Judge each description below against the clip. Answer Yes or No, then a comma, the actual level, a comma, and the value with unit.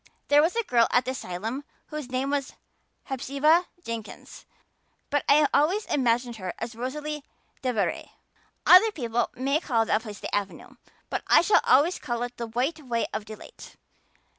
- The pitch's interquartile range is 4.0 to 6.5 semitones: Yes, average, 4.5 semitones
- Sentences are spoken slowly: No, average, 165 wpm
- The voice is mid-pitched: No, very high, 255 Hz